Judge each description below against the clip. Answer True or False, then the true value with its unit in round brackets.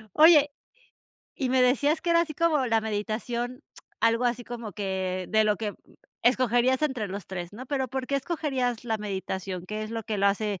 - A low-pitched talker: False (235 Hz)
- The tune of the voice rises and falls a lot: False (4.0 semitones)